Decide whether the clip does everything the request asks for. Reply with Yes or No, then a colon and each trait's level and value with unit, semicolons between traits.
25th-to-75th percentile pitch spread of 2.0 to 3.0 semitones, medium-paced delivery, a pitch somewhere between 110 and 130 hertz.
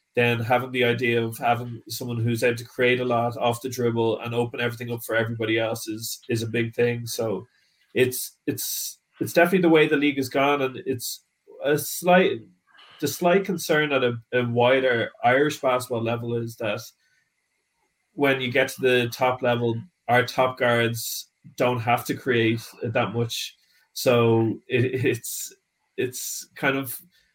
Yes: narrow, 2.5 semitones; average, 170 wpm; low, 125 Hz